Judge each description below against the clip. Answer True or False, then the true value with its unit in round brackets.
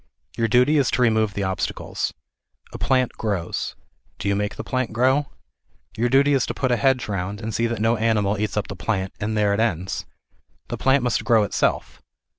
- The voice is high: False (110 Hz)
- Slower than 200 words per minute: False (205 wpm)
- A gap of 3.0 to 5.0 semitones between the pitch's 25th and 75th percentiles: True (3.5 semitones)